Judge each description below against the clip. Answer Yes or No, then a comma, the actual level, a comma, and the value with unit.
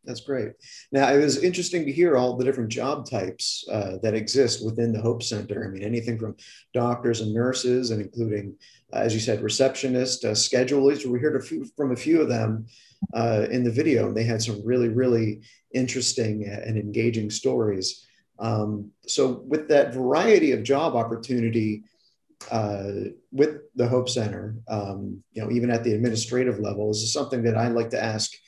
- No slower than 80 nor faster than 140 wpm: No, average, 185 wpm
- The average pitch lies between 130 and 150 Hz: No, low, 115 Hz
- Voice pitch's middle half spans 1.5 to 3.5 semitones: Yes, average, 2.7 semitones